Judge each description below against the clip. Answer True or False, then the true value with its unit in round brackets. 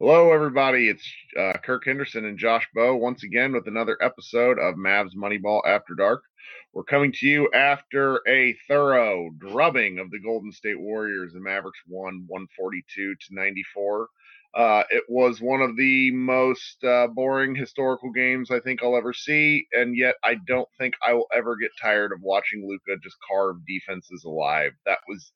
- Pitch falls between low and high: False (120 Hz)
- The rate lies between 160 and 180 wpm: True (175 wpm)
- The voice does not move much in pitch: False (4.8 semitones)